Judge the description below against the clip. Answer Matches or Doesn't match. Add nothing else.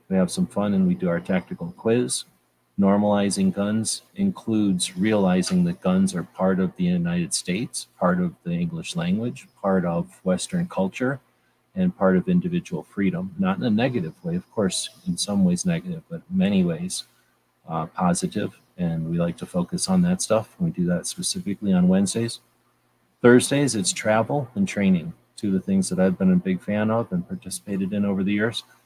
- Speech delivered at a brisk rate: Doesn't match